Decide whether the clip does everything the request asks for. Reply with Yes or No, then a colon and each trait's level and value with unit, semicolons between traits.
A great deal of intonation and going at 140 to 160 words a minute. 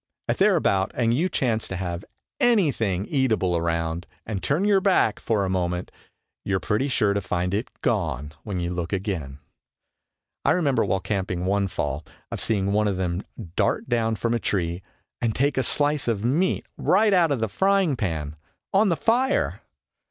No: wide, 7.4 semitones; average, 185 wpm